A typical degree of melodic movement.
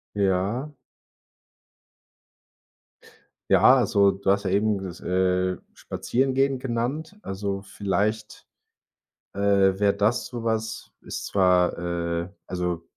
Yes: average, 3.7 semitones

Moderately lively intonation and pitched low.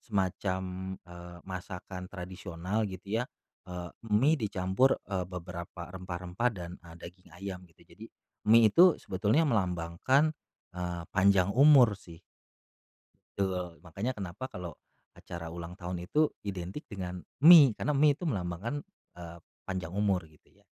Yes: average, 3.6 semitones; very low, 95 Hz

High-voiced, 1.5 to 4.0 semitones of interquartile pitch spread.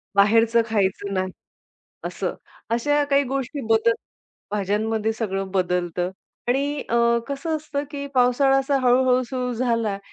No: high, 235 Hz; average, 4.7 semitones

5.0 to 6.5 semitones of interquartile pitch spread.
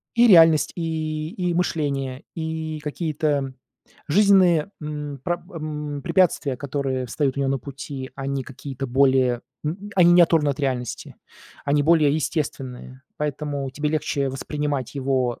No: average, 2.8 semitones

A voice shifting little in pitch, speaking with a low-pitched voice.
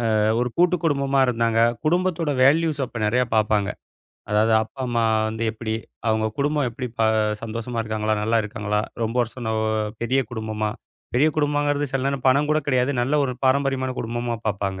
No: average, 4.2 semitones; low, 125 Hz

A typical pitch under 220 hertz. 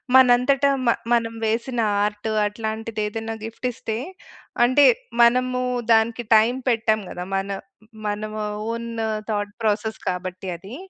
No: high, 225 Hz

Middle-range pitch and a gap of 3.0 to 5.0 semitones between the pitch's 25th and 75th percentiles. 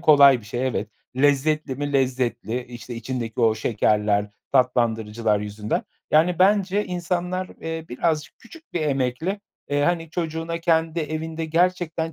No: medium, 145 Hz; wide, 5.5 semitones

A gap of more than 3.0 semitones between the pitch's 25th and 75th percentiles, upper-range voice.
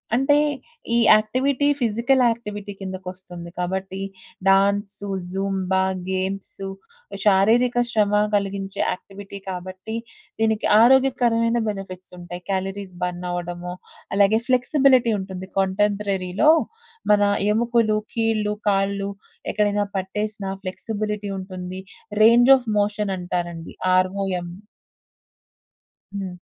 No: average, 2.7 semitones; high, 200 Hz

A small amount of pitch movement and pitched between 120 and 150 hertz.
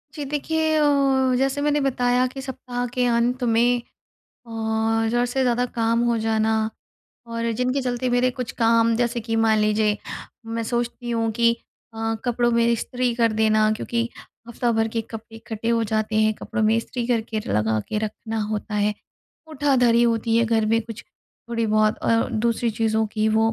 No: narrow, 1.7 semitones; high, 230 Hz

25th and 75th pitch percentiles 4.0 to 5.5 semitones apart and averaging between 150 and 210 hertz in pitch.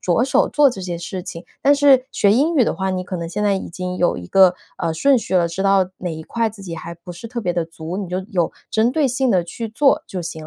Yes: average, 5.2 semitones; high, 190 Hz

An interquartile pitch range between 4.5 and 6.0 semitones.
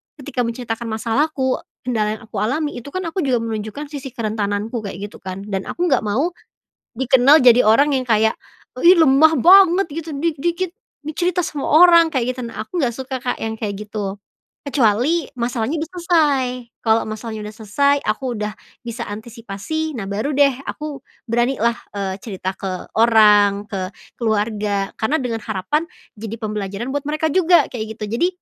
Yes: wide, 5.6 semitones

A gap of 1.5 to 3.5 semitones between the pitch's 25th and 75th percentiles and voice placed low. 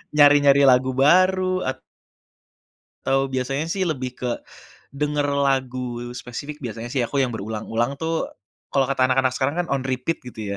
Yes: narrow, 2.5 semitones; low, 130 Hz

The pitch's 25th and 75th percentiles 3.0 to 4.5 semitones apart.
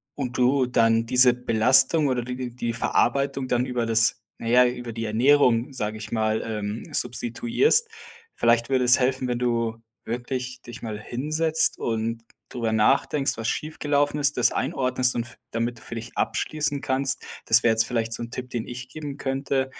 No: narrow, 2.6 semitones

